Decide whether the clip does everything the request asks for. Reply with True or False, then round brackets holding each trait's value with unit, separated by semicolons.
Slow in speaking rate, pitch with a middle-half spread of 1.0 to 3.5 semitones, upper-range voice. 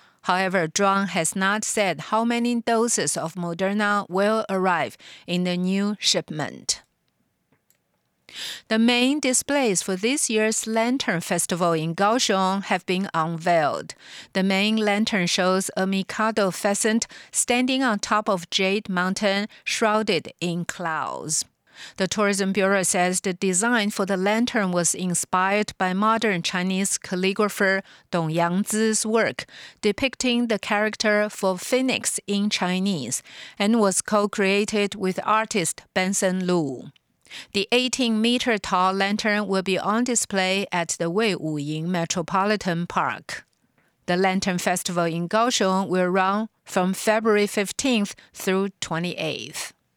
True (125 wpm; 2.8 semitones; 195 Hz)